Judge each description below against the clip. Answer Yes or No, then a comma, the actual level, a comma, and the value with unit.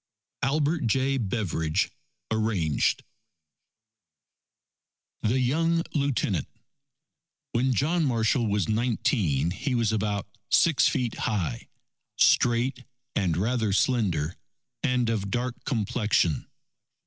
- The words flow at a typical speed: No, slow, 90 wpm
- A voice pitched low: Yes, low, 115 Hz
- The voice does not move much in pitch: No, average, 4.4 semitones